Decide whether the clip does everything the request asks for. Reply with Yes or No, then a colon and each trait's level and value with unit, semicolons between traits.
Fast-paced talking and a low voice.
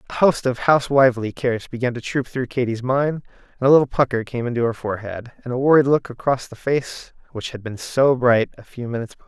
Yes: fast, 225 wpm; low, 125 Hz